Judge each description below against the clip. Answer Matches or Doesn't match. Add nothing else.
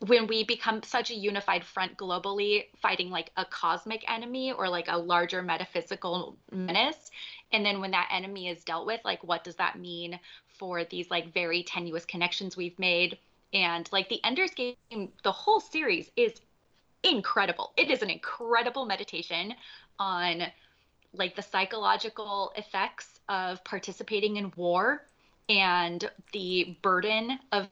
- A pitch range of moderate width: Matches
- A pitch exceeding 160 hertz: Matches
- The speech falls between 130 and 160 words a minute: Matches